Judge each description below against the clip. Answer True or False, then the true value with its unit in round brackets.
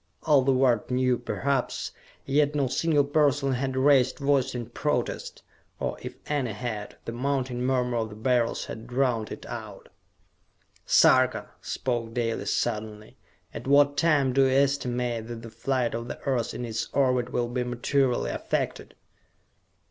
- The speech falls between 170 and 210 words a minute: False (155 wpm)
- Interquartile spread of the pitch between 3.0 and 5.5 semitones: False (2.6 semitones)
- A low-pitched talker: True (125 Hz)